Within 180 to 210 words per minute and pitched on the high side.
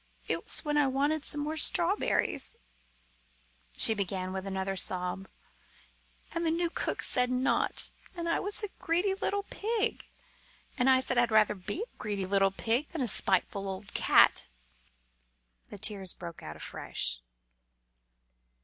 No: average, 155 wpm; high, 245 Hz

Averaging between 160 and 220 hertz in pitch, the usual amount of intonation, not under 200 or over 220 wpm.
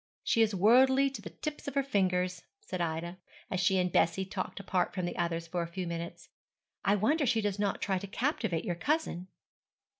Yes: high, 190 Hz; average, 4.6 semitones; fast, 205 wpm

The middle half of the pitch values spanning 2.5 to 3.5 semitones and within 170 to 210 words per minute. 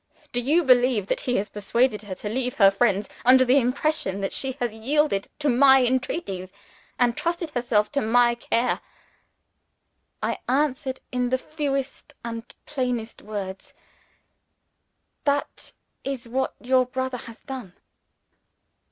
No: average, 3.2 semitones; slow, 135 wpm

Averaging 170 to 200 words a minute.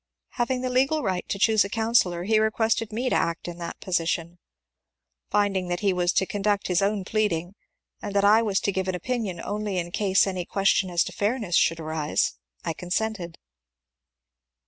Yes: average, 190 wpm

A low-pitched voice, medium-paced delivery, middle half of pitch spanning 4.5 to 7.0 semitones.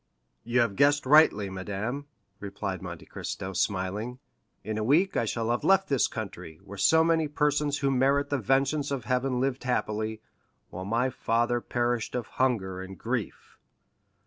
Yes: low, 120 Hz; average, 160 wpm; average, 4.8 semitones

